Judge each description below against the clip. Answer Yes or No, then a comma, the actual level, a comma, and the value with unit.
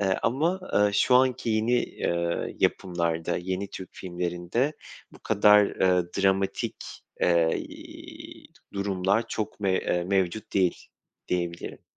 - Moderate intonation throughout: Yes, average, 3.3 semitones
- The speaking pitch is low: Yes, very low, 95 Hz